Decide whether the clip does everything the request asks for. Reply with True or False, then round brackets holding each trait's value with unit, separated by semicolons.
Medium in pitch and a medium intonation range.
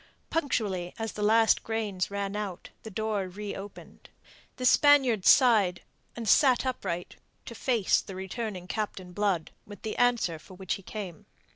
False (210 Hz; 3.3 semitones)